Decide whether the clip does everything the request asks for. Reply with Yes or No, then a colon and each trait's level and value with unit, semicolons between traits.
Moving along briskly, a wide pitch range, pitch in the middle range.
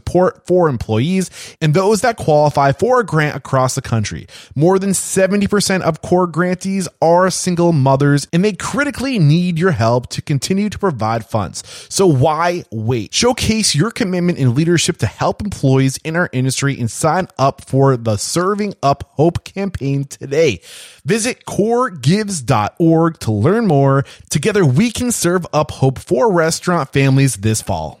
No: average, 155 wpm; wide, 5.8 semitones; medium, 160 Hz